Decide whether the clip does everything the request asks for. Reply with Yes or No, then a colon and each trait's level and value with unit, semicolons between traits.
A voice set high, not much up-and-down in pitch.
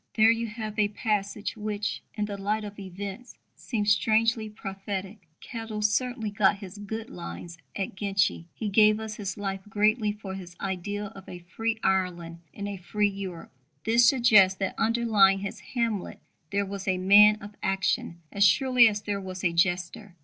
Yes: high, 205 Hz; narrow, 2.1 semitones